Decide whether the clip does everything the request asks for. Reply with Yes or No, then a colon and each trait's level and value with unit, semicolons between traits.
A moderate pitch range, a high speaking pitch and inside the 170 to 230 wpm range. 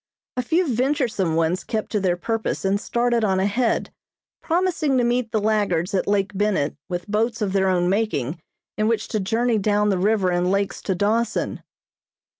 Yes: average, 3.6 semitones; high, 210 Hz; average, 180 wpm